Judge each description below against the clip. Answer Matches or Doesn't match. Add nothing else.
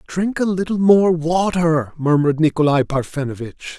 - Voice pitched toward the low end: Doesn't match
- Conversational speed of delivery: Doesn't match